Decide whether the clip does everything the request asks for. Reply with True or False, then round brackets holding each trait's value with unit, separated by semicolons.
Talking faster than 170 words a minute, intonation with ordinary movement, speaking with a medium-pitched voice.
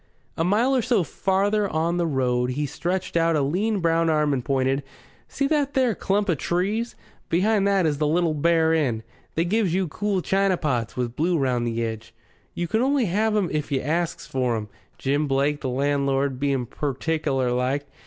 False (195 wpm; 6.1 semitones; 160 Hz)